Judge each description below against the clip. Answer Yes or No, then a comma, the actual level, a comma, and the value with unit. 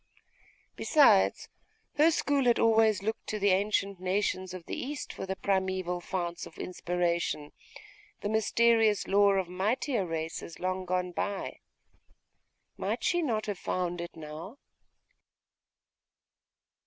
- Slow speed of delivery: Yes, slow, 125 wpm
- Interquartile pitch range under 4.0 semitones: Yes, average, 3.6 semitones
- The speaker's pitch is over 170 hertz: Yes, high, 190 Hz